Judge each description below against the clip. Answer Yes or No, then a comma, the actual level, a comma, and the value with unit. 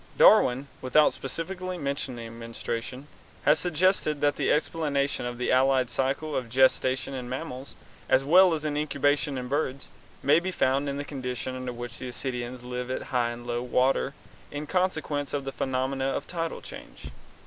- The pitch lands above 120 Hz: Yes, low, 135 Hz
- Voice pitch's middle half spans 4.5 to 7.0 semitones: No, average, 2.9 semitones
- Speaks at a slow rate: No, average, 160 wpm